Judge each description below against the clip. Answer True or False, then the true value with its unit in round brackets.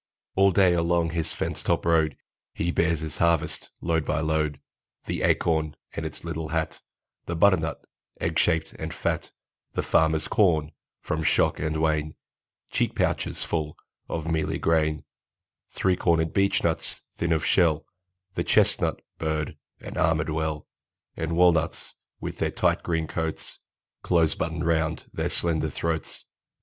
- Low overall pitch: True (80 Hz)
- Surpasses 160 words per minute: False (145 wpm)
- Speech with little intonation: True (1.2 semitones)